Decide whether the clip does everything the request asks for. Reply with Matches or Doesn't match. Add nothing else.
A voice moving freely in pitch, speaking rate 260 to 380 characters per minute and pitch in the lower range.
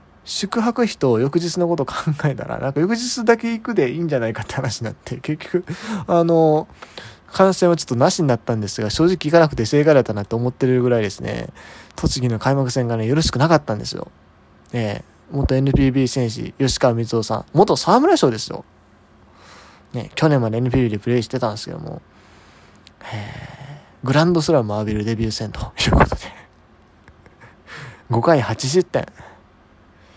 Matches